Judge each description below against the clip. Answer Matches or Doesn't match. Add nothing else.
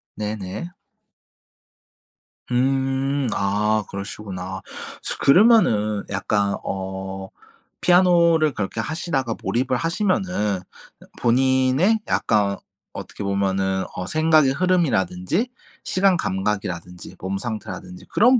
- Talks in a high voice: Doesn't match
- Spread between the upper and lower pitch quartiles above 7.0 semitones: Matches